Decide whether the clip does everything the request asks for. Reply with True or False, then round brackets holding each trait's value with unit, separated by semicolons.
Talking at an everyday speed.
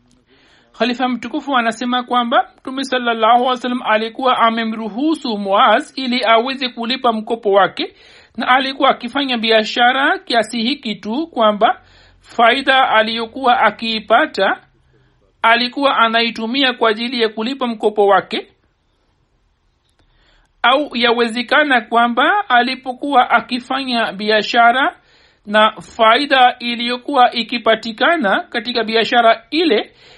False (95 wpm)